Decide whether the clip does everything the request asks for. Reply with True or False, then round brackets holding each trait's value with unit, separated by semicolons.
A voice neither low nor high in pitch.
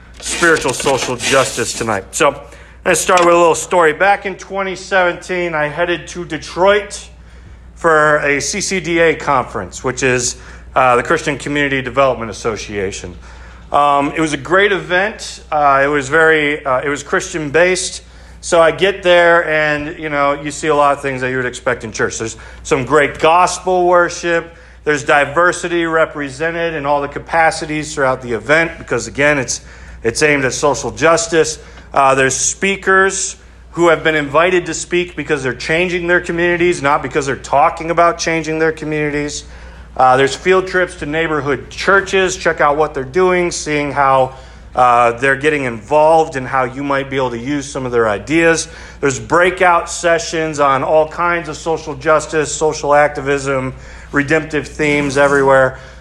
True (150 Hz)